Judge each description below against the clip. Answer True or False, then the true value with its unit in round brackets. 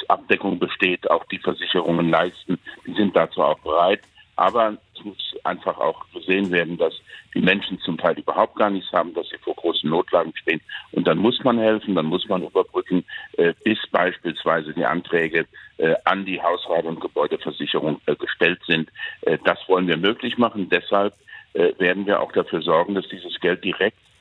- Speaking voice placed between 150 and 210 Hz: False (120 Hz)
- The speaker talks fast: False (170 wpm)